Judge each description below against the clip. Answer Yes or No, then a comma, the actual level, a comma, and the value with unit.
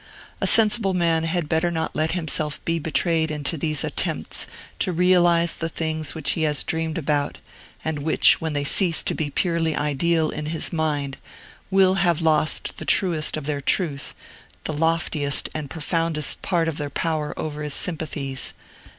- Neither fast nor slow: Yes, average, 170 wpm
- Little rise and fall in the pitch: Yes, narrow, 2.0 semitones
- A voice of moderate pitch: Yes, medium, 160 Hz